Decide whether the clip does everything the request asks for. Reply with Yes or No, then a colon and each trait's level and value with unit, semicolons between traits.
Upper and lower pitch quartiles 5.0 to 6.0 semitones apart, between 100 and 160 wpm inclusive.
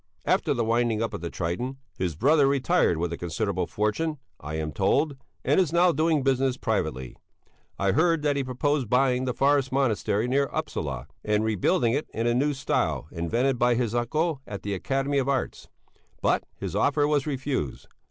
No: wide, 5.5 semitones; average, 180 wpm